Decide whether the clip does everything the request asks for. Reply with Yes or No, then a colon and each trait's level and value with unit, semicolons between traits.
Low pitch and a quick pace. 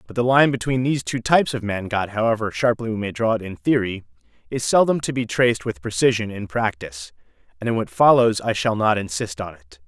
Yes: low, 110 Hz; fast, 225 wpm